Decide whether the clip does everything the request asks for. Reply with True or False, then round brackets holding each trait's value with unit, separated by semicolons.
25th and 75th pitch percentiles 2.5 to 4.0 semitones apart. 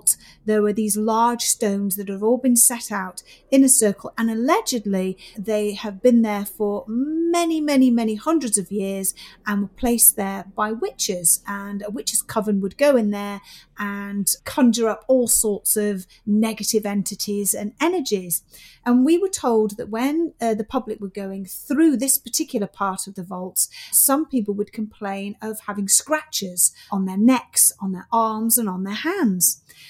True (3.3 semitones)